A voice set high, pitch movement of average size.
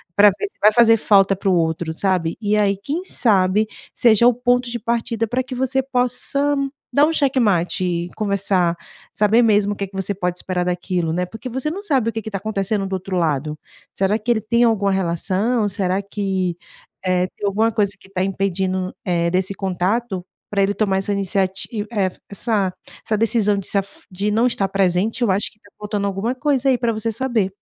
Yes: high, 200 Hz; average, 3.4 semitones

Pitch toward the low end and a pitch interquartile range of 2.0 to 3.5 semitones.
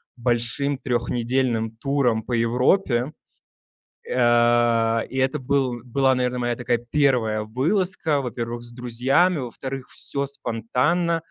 Yes: low, 125 Hz; narrow, 2.6 semitones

